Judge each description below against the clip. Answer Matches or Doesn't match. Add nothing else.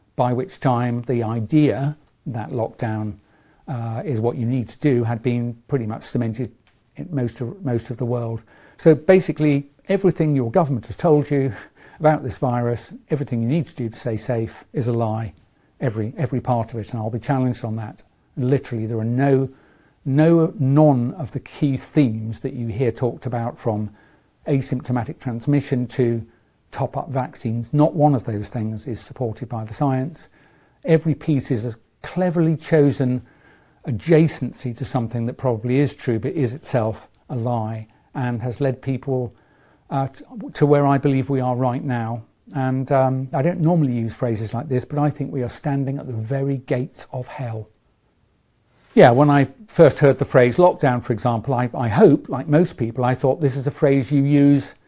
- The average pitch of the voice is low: Matches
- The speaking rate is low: Doesn't match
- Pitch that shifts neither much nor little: Matches